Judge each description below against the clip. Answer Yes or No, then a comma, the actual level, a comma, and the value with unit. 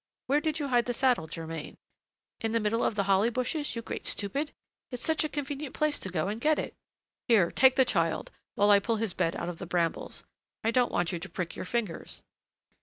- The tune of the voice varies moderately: No, wide, 6.4 semitones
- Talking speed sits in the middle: No, fast, 225 wpm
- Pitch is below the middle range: No, high, 230 Hz